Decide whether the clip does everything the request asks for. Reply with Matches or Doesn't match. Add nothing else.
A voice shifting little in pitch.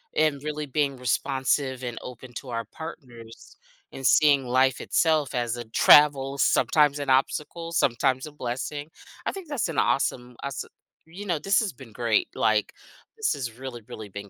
Doesn't match